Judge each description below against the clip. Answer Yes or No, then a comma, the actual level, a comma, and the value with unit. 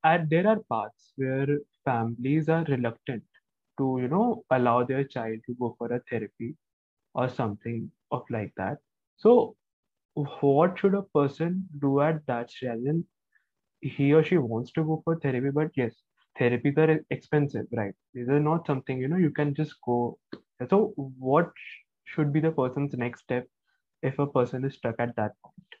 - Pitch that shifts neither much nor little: Yes, average, 4.2 semitones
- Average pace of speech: Yes, average, 170 wpm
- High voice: No, low, 135 Hz